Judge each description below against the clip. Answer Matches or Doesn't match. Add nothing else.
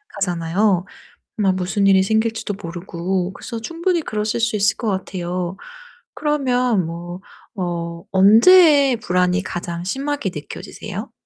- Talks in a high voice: Matches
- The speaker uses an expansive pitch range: Doesn't match